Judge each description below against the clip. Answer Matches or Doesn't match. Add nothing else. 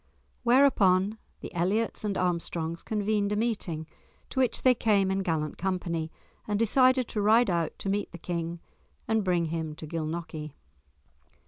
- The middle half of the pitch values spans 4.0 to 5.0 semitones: Matches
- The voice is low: Doesn't match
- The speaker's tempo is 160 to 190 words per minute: Doesn't match